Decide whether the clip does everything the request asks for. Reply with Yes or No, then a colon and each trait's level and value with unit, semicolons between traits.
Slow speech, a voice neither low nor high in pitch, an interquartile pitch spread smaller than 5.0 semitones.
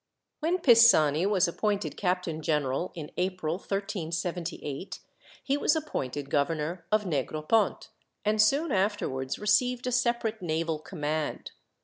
No: slow, 115 wpm; medium, 180 Hz; wide, 5.6 semitones